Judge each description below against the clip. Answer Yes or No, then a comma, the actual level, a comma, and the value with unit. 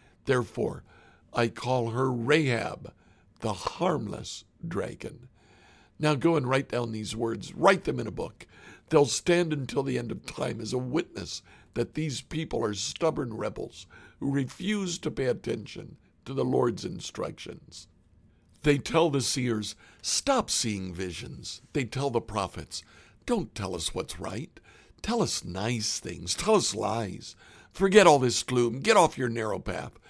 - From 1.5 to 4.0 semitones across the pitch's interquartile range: No, wide, 5.6 semitones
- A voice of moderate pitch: No, low, 120 Hz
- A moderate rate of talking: Yes, average, 155 wpm